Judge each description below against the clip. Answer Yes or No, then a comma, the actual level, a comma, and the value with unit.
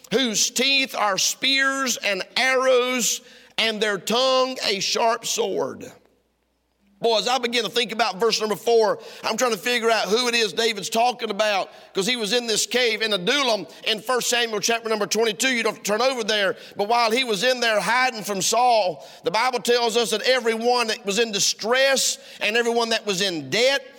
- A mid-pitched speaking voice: No, high, 235 Hz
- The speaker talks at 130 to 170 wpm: No, average, 195 wpm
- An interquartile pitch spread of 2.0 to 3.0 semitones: Yes, average, 2.7 semitones